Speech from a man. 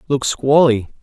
Yes: male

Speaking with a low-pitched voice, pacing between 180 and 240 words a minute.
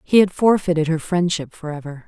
No: medium, 170 Hz; fast, 205 wpm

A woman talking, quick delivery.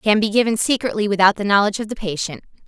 Yes: female; fast, 225 wpm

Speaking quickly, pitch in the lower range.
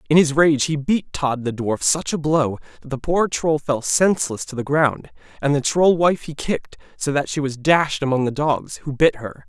No: fast, 235 wpm; medium, 145 Hz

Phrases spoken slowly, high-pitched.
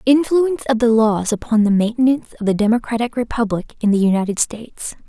No: average, 175 wpm; high, 230 Hz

